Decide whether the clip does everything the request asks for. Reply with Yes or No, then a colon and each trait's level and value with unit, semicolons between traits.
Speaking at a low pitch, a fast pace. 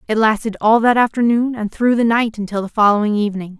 No: high, 220 Hz; fast, 215 wpm